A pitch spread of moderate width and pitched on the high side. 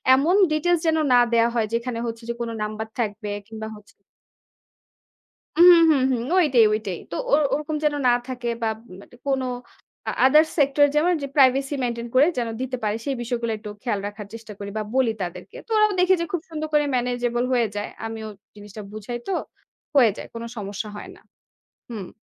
Yes: average, 4.3 semitones; high, 240 Hz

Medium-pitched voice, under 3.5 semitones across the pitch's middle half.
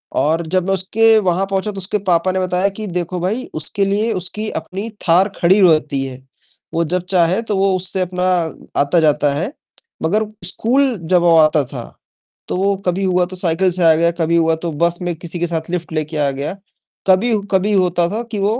Yes: medium, 180 Hz; average, 2.9 semitones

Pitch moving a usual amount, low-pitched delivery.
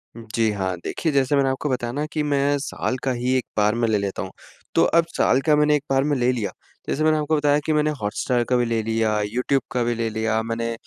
Yes: average, 4.2 semitones; low, 125 Hz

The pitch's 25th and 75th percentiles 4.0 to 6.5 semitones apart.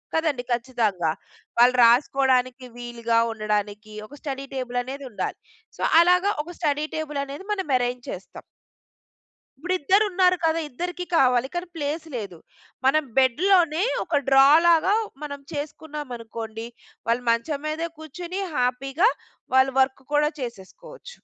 Yes: average, 4.8 semitones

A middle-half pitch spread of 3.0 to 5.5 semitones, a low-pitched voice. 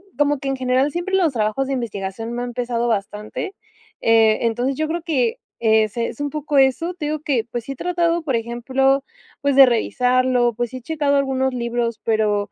No: average, 3.5 semitones; very high, 255 Hz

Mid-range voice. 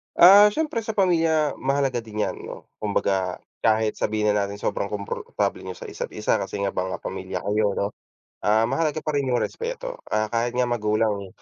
No: low, 115 Hz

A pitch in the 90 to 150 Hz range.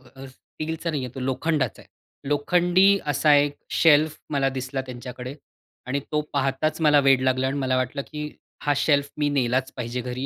Yes: medium, 140 Hz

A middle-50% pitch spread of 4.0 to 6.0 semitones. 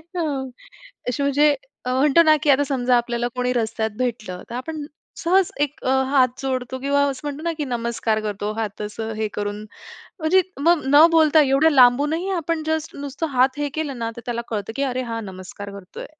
Yes: average, 4.3 semitones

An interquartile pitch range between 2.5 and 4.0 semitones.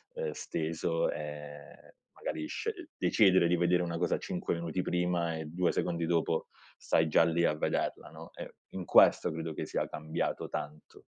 No: narrow, 2.0 semitones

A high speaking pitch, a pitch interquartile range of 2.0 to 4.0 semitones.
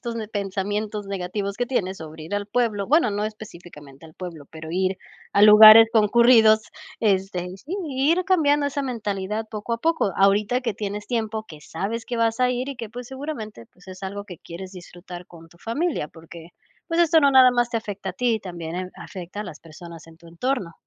No: high, 205 Hz; average, 4.7 semitones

